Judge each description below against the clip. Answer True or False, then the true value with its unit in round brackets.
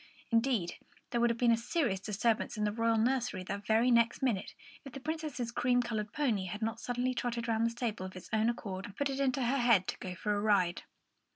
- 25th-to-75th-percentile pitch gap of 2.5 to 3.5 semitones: True (2.8 semitones)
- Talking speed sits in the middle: False (240 wpm)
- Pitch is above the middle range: True (230 Hz)